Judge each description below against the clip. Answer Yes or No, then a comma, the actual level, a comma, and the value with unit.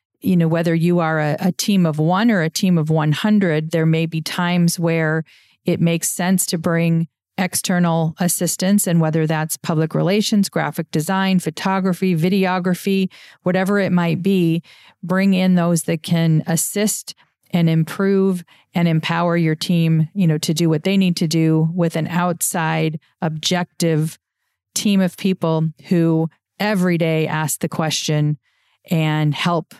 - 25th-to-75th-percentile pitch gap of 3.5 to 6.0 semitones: No, narrow, 2.5 semitones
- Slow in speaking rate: No, average, 155 wpm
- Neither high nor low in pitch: Yes, medium, 170 Hz